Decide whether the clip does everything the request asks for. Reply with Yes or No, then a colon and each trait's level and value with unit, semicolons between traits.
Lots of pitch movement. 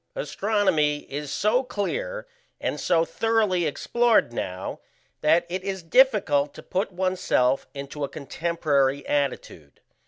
Yes: wide, 6.5 semitones